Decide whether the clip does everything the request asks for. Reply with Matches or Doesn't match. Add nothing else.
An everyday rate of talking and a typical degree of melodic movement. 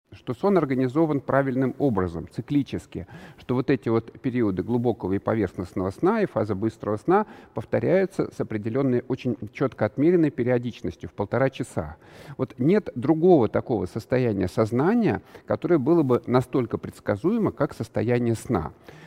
Matches